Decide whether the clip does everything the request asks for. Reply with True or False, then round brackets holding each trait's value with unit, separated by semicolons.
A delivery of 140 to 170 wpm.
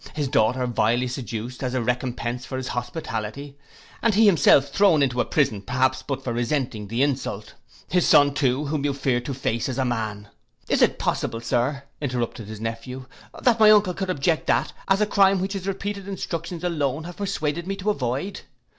False (190 wpm)